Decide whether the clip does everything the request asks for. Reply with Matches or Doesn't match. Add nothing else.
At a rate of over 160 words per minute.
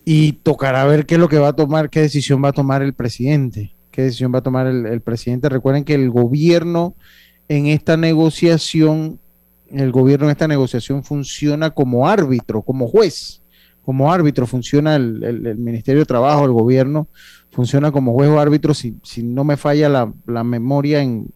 Matches